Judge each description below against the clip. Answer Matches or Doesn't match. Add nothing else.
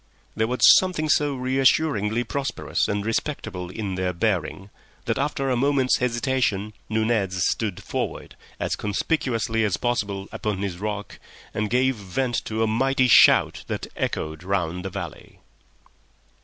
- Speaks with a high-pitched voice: Doesn't match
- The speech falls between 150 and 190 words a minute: Doesn't match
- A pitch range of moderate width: Matches